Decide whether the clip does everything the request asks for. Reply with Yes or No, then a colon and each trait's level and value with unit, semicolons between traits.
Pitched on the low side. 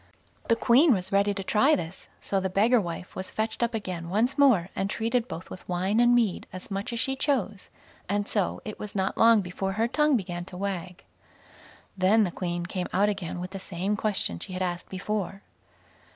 No: high, 200 Hz